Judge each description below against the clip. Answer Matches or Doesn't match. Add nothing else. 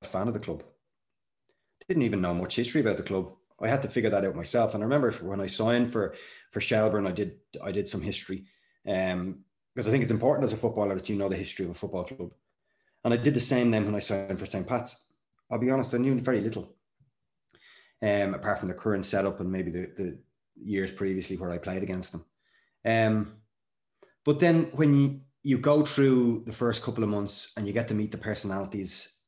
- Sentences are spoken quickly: Matches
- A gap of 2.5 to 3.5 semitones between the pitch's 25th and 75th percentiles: Doesn't match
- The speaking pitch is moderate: Doesn't match